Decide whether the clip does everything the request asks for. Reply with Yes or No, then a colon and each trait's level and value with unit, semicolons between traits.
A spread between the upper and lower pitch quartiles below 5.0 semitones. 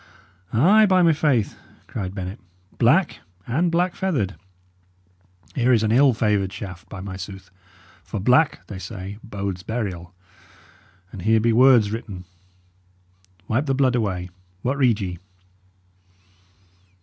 No: average, 5.3 semitones